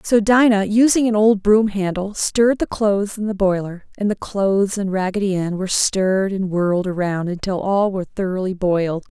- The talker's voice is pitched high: Yes, high, 200 Hz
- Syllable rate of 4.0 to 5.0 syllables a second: No, 5.3 syllables/s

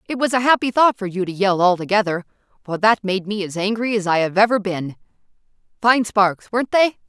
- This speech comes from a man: No, female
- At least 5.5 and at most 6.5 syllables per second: Yes, 5.7 syllables/s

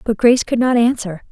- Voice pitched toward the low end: No, high, 230 Hz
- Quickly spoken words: Yes, fast, 230 wpm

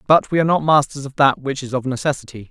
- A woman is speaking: No, male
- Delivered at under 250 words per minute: No, fast, 265 wpm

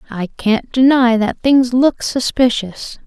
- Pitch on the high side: Yes, high, 240 Hz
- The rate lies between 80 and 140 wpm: Yes, slow, 135 wpm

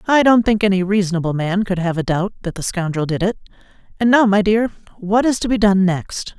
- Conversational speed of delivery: No, fast, 235 wpm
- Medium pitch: No, high, 200 Hz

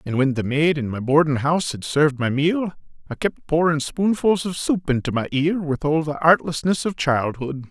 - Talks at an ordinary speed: No, fast, 210 wpm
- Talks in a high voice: No, medium, 150 Hz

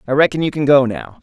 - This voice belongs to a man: Yes, male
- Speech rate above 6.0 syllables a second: Yes, 6.5 syllables/s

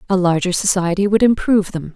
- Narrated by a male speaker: No, female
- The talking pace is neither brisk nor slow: Yes, average, 185 wpm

